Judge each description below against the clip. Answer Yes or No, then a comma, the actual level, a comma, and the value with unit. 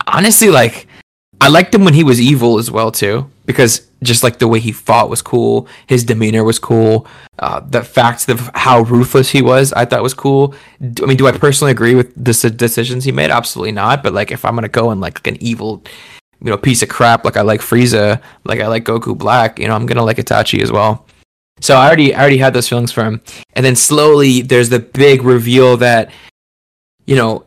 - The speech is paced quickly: Yes, fast, 225 wpm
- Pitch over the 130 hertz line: No, low, 120 Hz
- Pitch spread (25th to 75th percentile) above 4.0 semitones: No, average, 2.7 semitones